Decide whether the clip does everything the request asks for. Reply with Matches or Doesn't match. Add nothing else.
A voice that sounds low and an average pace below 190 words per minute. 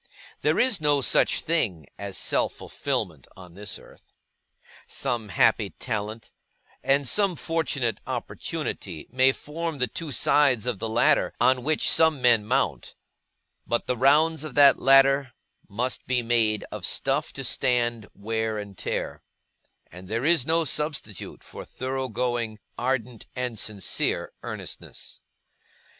Matches